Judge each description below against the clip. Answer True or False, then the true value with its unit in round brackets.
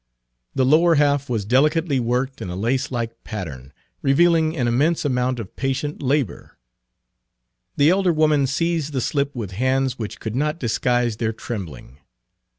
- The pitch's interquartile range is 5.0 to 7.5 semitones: False (4.3 semitones)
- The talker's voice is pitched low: True (130 Hz)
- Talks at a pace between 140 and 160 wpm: True (150 wpm)